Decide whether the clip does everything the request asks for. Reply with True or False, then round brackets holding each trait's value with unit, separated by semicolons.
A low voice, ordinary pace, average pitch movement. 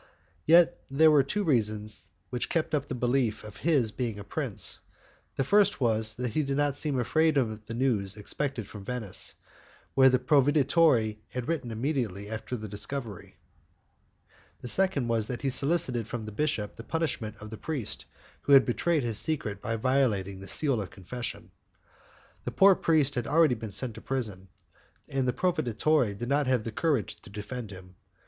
True (125 Hz; 175 wpm; 5.0 semitones)